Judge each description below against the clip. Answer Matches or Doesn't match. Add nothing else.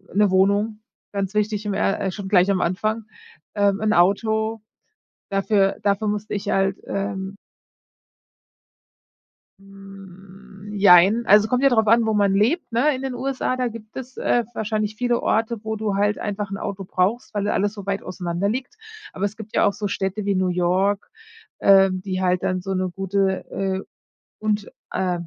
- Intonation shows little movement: Matches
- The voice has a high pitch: Matches